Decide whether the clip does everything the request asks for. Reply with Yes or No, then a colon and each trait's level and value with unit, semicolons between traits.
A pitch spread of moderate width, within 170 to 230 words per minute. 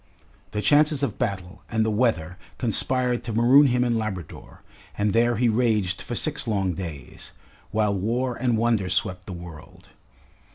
No: average, 4.4 semitones; average, 160 wpm